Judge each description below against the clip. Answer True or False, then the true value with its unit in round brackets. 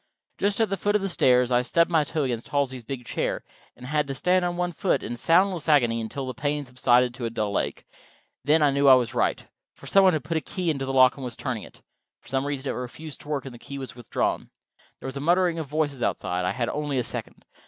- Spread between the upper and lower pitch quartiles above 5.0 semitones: False (4.3 semitones)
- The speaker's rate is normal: False (260 wpm)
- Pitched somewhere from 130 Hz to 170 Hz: True (140 Hz)